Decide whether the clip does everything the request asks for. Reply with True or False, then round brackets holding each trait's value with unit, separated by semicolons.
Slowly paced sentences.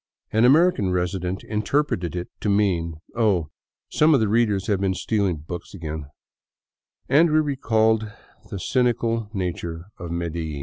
False (165 wpm)